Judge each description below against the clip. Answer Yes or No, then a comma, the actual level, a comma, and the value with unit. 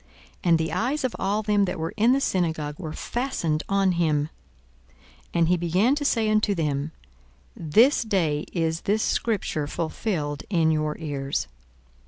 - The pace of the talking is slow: No, average, 160 wpm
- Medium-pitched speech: Yes, medium, 175 Hz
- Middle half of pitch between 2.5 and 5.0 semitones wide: No, wide, 5.5 semitones